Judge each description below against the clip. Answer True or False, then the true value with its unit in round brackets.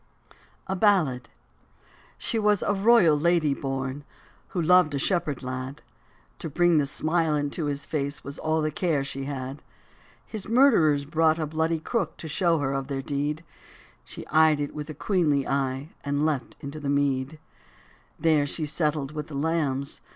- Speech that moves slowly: False (170 wpm)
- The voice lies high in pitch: False (150 Hz)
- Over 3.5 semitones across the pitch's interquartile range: False (2.8 semitones)